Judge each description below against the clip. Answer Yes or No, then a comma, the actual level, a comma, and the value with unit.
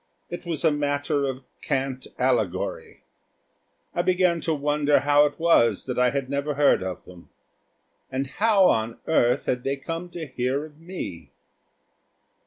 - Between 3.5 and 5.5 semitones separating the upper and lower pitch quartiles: Yes, average, 4.0 semitones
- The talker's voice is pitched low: No, medium, 145 Hz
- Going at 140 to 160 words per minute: Yes, average, 155 wpm